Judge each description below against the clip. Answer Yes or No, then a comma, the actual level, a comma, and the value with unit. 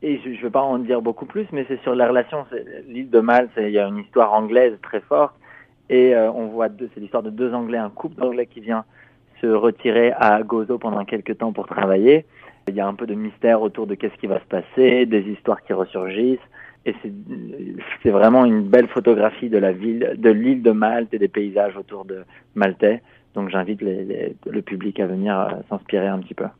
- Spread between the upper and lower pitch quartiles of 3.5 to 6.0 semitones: No, average, 3.1 semitones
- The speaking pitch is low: Yes, low, 115 Hz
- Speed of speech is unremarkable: No, fast, 230 wpm